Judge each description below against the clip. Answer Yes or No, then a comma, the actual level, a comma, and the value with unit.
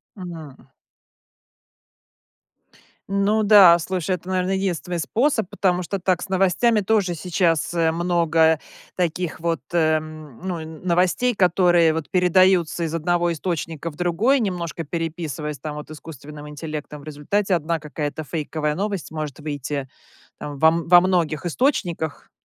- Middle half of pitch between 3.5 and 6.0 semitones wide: No, average, 2.9 semitones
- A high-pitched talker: No, medium, 170 Hz